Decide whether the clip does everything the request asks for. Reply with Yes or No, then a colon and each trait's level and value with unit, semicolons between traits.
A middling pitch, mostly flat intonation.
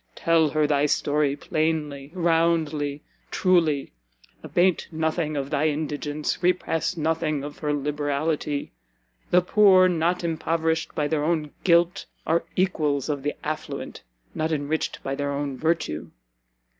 Yes: medium, 155 Hz; narrow, 2.2 semitones